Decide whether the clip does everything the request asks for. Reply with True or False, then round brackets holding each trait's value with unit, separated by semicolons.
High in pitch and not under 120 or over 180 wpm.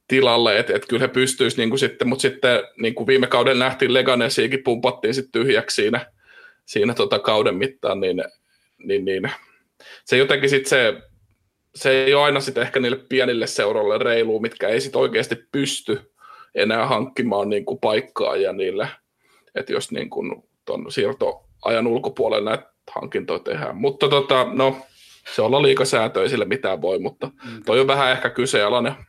True (400 Hz; 150 wpm)